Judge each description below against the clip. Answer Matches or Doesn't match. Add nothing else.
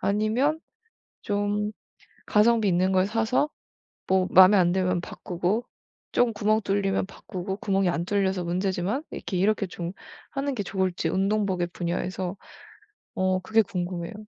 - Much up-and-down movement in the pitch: Doesn't match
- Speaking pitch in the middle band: Doesn't match